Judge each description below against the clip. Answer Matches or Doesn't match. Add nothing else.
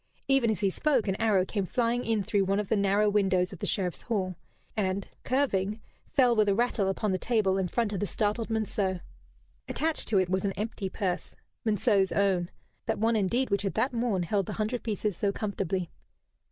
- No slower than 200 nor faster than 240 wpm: Matches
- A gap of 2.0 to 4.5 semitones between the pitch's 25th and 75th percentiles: Matches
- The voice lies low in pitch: Doesn't match